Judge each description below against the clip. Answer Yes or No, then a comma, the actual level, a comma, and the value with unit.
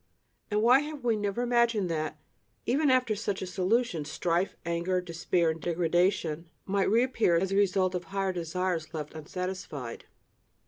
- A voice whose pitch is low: No, medium, 185 Hz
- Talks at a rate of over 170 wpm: No, average, 150 wpm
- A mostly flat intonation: No, average, 4.2 semitones